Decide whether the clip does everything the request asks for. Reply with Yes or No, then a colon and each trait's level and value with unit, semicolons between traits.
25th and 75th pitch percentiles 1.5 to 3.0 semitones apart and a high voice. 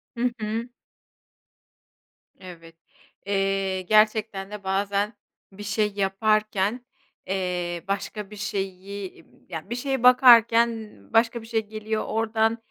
Yes: narrow, 2.5 semitones; high, 210 Hz